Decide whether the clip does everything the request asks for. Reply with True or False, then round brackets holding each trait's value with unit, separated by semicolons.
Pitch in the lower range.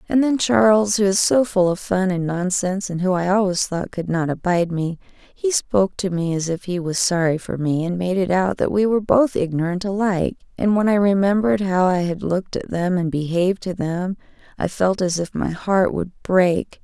False (185 Hz)